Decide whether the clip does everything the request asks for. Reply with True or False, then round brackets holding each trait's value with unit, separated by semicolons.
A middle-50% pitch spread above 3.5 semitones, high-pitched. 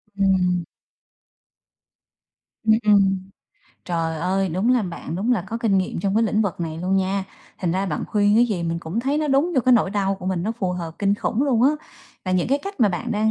True (3.9 semitones; 195 Hz)